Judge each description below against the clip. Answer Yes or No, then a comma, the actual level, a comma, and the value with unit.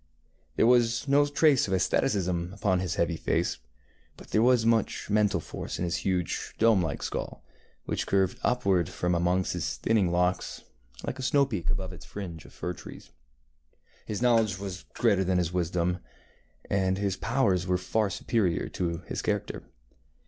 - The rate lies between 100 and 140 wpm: No, average, 165 wpm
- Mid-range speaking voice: No, very low, 95 Hz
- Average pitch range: Yes, average, 4.0 semitones